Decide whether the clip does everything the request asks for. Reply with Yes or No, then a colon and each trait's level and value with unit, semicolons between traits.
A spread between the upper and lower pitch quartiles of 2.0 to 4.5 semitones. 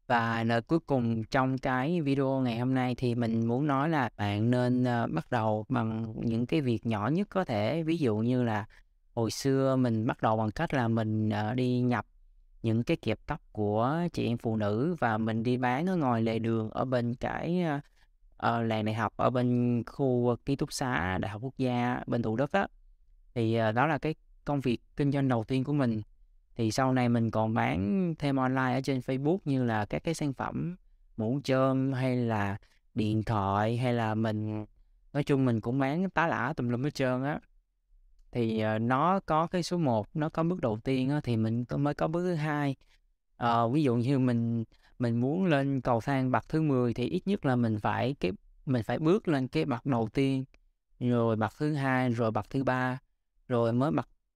Yes: average, 3.7 semitones